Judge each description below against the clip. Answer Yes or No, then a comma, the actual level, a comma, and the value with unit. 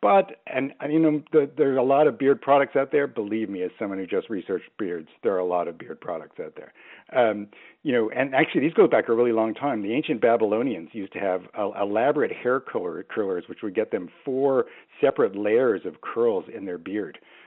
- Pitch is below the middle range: No, medium, 145 Hz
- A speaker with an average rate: No, fast, 230 wpm